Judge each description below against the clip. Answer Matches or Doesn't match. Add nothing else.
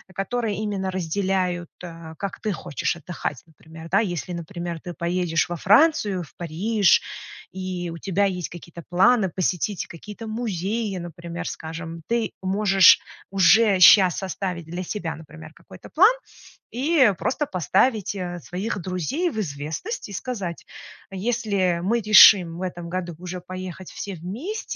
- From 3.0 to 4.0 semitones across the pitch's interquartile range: Matches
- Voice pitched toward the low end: Doesn't match